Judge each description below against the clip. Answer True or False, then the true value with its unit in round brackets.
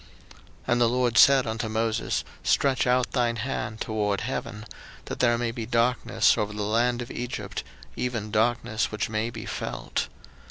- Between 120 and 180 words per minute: True (165 wpm)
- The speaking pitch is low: True (115 Hz)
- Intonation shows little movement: True (2.0 semitones)